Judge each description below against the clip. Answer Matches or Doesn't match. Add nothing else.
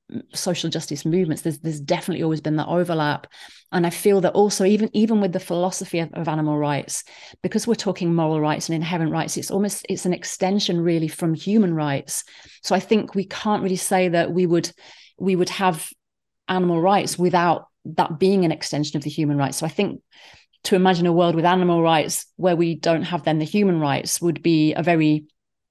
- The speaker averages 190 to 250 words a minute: Matches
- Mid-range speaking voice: Matches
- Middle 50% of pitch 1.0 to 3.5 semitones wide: Matches